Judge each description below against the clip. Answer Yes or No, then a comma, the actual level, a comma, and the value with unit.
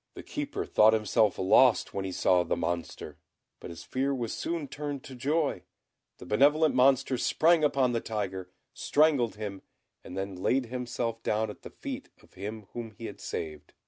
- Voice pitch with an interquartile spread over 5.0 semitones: Yes, wide, 5.5 semitones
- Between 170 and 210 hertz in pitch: No, low, 115 Hz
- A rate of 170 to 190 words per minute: Yes, average, 175 wpm